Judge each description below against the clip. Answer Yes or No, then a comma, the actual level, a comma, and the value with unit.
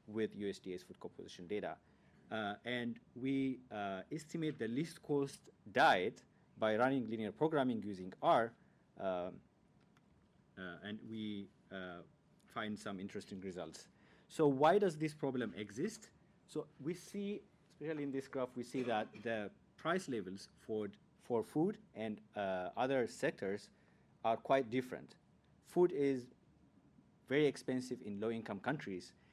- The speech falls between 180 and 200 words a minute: No, slow, 135 wpm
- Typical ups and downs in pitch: No, wide, 6.2 semitones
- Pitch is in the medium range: No, low, 125 Hz